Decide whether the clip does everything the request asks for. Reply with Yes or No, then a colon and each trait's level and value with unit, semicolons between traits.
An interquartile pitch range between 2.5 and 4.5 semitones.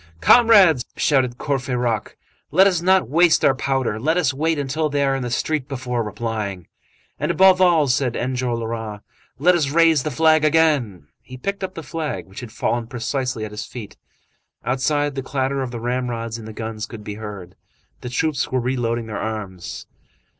No: average, 5.0 semitones